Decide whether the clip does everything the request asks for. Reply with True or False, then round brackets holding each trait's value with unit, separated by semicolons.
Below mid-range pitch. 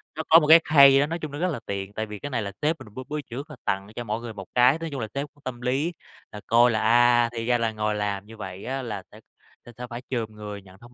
True (120 Hz)